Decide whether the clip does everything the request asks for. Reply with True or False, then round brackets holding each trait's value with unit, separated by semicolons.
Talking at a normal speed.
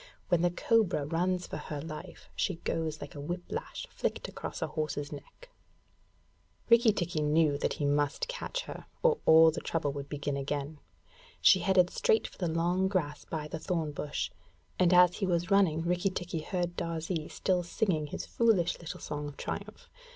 True (180 wpm)